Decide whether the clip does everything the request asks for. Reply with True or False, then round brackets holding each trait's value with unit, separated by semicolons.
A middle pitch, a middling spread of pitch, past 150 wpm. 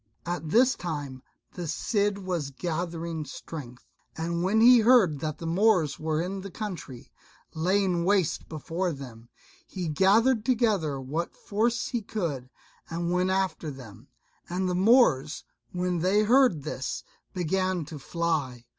False (175 Hz; 4.4 semitones; 140 wpm)